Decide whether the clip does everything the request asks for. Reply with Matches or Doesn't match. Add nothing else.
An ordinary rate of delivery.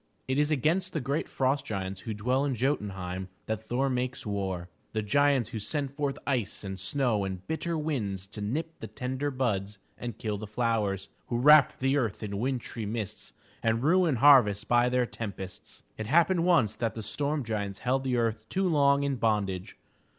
Matches